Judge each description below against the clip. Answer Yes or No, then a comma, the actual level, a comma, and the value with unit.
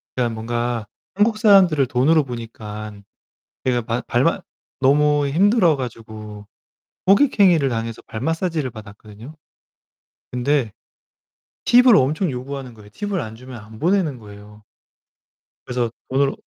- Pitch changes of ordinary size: No, wide, 6.2 semitones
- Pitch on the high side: No, low, 130 Hz